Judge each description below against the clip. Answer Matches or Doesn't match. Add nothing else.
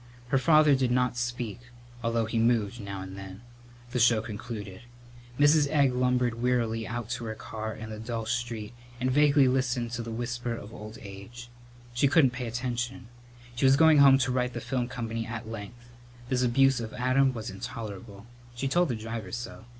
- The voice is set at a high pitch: Doesn't match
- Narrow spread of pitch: Matches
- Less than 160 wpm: Doesn't match